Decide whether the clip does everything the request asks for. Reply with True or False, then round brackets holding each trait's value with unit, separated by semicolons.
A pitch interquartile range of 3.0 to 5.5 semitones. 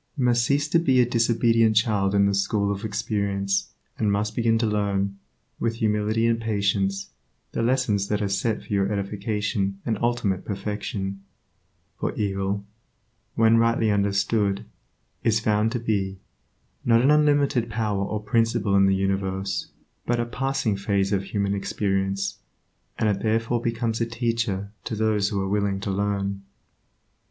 False (2.6 semitones)